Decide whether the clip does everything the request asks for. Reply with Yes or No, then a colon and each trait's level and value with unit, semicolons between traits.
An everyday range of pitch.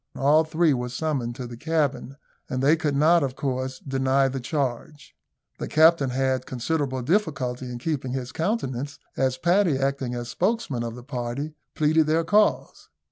Yes: average, 3.6 semitones